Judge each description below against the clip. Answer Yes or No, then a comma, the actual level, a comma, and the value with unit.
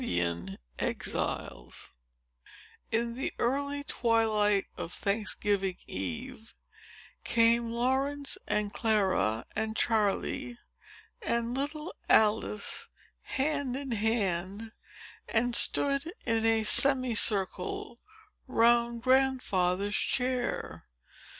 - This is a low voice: No, high, 230 Hz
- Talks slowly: Yes, slow, 85 wpm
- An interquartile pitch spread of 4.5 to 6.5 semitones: No, average, 3.9 semitones